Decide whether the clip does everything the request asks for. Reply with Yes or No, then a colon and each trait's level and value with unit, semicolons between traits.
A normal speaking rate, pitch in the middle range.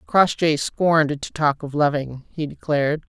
Yes: average, 155 wpm; medium, 150 Hz